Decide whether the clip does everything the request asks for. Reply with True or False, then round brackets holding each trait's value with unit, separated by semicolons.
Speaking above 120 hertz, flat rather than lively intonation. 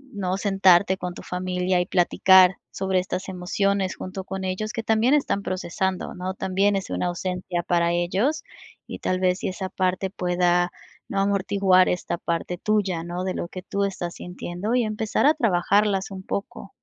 True (185 Hz; 1.7 semitones)